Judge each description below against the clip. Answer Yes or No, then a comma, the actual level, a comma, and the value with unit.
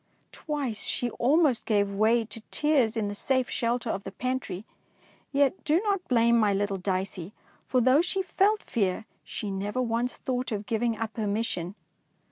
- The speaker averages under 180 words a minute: Yes, average, 170 wpm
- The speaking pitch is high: Yes, high, 230 Hz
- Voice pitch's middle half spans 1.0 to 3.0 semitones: No, average, 4.1 semitones